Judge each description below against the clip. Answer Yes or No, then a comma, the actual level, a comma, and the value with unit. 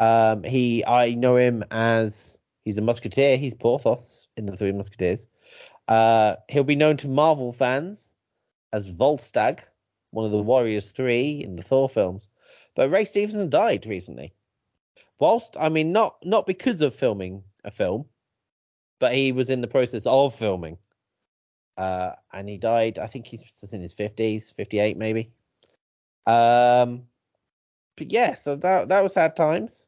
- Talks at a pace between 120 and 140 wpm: No, average, 155 wpm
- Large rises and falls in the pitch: No, average, 4.6 semitones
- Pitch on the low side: Yes, low, 120 Hz